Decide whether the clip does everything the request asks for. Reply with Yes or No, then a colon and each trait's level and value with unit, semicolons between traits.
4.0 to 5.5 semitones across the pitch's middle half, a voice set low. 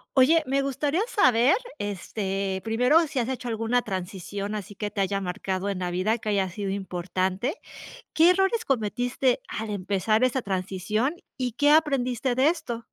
No: average, 5.1 semitones; high, 225 Hz